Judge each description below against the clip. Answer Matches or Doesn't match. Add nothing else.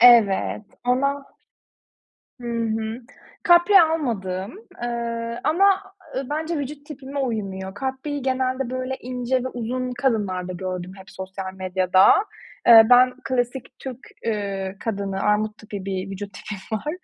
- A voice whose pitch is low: Doesn't match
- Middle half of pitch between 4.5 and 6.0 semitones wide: Matches